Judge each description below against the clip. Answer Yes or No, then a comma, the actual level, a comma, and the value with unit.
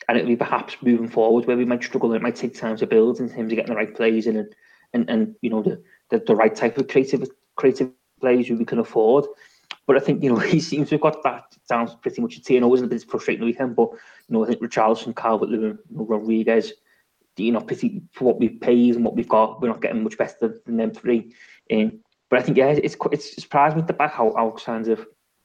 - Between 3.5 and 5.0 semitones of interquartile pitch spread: Yes, average, 4.1 semitones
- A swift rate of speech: Yes, fast, 260 wpm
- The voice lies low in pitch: Yes, low, 120 Hz